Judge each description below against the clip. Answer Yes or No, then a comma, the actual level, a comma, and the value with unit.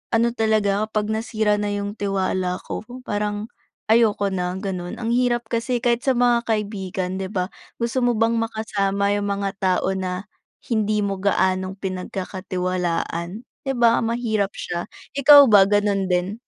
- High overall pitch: Yes, high, 205 Hz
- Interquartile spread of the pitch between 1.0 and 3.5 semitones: Yes, average, 3.1 semitones